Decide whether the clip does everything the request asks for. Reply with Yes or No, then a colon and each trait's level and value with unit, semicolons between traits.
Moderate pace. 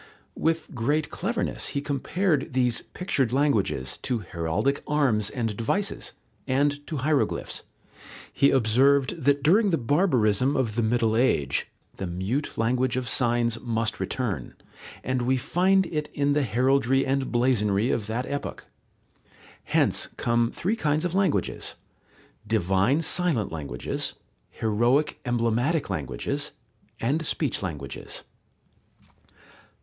No: slow, 120 wpm